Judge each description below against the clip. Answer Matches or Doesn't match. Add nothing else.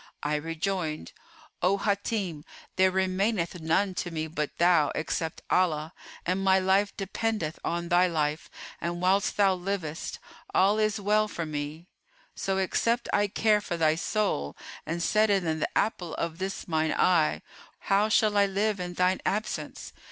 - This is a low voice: Doesn't match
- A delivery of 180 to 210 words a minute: Doesn't match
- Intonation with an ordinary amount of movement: Matches